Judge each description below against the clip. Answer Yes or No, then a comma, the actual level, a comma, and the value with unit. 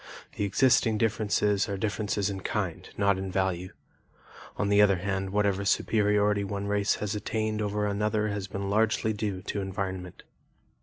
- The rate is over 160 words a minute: No, average, 155 wpm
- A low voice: Yes, low, 100 Hz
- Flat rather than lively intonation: Yes, narrow, 1.3 semitones